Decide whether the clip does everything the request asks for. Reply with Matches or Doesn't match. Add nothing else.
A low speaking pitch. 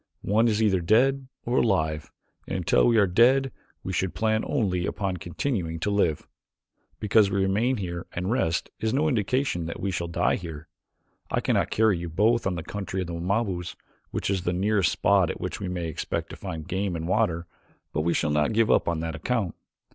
Matches